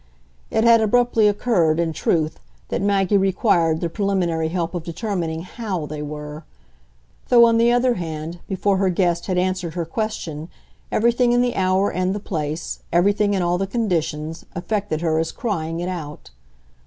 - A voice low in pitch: No, medium, 180 Hz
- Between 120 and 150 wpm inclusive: No, average, 165 wpm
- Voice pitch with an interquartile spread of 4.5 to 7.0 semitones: No, average, 4.1 semitones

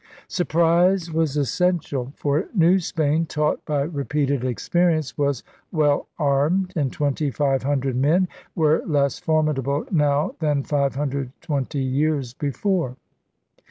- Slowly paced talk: Yes, slow, 125 wpm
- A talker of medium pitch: Yes, medium, 145 Hz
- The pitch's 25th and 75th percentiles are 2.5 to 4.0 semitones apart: Yes, average, 2.8 semitones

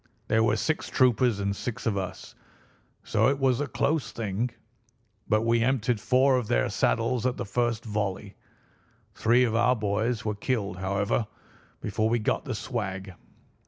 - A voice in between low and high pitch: No, low, 115 Hz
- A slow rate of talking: No, average, 160 wpm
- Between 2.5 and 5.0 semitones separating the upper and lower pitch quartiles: Yes, average, 3.5 semitones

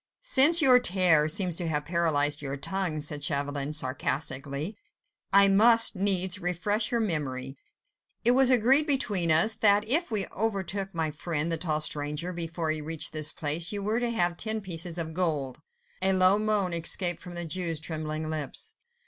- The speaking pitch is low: No, medium, 175 Hz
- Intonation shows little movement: No, average, 4.9 semitones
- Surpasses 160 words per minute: Yes, average, 170 wpm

